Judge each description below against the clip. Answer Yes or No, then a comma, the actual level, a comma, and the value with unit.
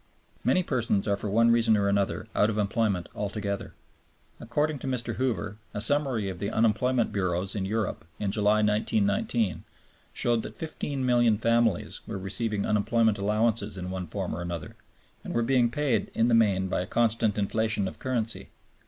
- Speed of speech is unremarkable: Yes, average, 170 wpm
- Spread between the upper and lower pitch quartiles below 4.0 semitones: Yes, average, 2.8 semitones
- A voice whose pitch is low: Yes, low, 110 Hz